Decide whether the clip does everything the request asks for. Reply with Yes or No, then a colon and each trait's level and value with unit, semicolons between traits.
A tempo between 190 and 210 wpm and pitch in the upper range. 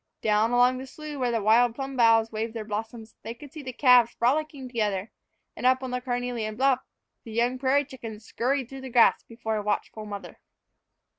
Yes: average, 200 wpm; high, 240 Hz